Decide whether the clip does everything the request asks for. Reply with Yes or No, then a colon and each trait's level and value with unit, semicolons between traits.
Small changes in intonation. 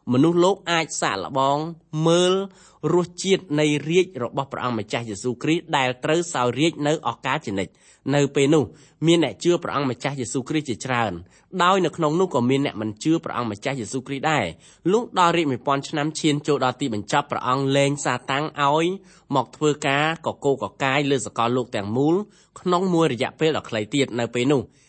No: average, 4.3 semitones